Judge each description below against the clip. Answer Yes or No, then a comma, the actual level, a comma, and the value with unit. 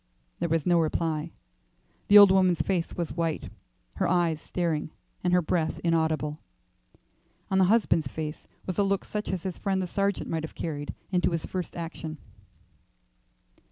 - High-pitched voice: No, medium, 170 Hz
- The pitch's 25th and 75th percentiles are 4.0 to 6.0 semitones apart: No, average, 2.7 semitones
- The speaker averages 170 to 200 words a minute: No, average, 160 wpm